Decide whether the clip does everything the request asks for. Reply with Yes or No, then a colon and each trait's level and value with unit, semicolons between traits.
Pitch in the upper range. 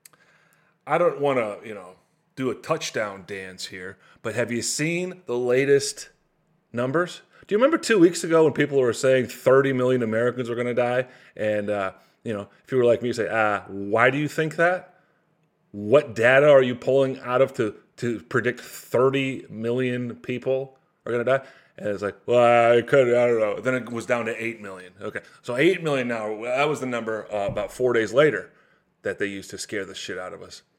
No: low, 125 Hz